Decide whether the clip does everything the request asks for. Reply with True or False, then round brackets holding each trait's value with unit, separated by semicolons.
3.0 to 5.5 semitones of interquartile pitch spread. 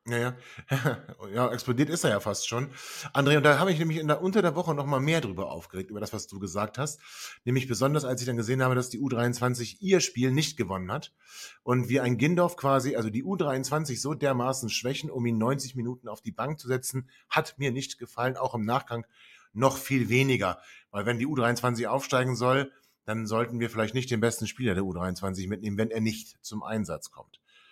True (3.3 semitones)